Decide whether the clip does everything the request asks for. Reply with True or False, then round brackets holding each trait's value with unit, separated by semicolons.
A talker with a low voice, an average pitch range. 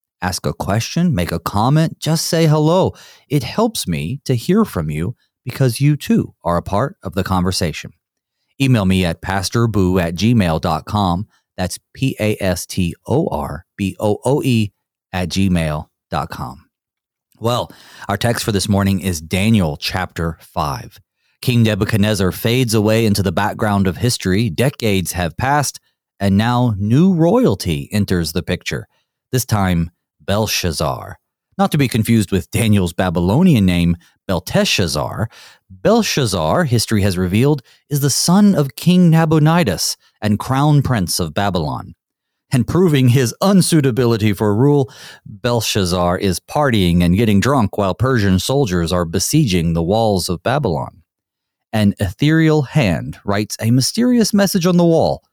False (110 Hz; 7.1 semitones)